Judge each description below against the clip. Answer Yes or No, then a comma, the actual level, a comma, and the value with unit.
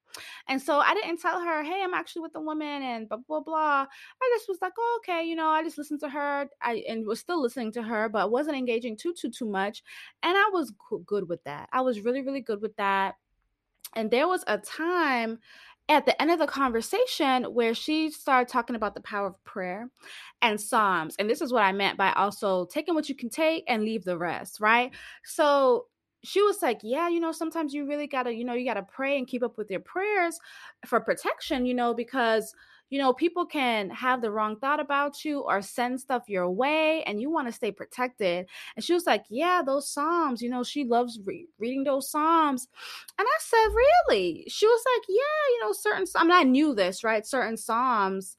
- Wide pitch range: Yes, wide, 6.4 semitones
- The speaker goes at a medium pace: No, fast, 220 wpm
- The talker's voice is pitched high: Yes, very high, 270 Hz